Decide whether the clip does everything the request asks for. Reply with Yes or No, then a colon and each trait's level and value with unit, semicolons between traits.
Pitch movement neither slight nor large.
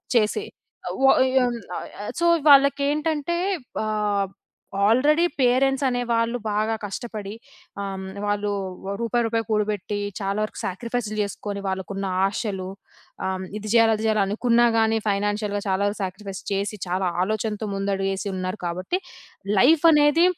Yes: average, 3.6 semitones